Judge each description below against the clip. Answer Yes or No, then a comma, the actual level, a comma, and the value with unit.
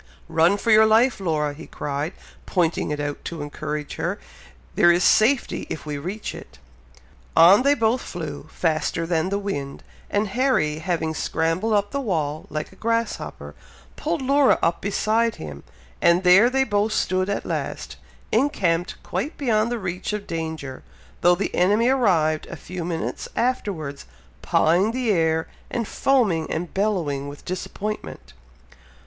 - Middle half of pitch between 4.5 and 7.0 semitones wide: Yes, wide, 5.5 semitones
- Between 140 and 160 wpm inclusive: Yes, average, 155 wpm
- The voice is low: No, medium, 180 Hz